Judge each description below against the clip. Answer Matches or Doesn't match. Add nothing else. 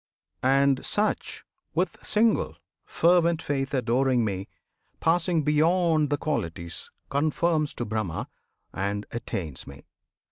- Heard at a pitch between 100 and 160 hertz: Matches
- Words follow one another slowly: Matches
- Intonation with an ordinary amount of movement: Doesn't match